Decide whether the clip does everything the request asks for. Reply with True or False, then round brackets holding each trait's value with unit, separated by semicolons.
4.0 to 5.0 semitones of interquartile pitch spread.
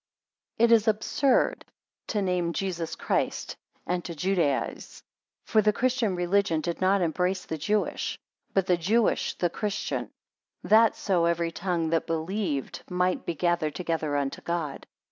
False (3.3 semitones)